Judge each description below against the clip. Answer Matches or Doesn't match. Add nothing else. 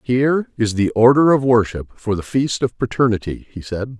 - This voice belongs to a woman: Doesn't match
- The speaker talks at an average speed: Matches